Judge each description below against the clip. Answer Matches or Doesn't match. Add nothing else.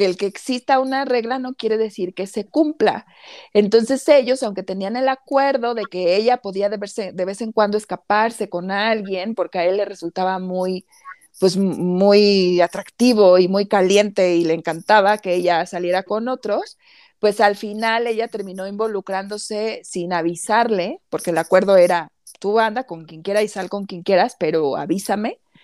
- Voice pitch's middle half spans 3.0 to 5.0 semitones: Matches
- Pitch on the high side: Matches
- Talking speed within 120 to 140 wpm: Doesn't match